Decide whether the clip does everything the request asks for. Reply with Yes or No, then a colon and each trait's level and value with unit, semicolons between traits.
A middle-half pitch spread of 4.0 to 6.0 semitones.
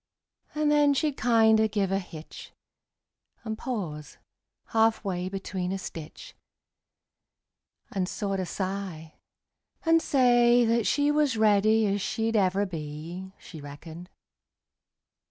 Yes: average, 4.5 semitones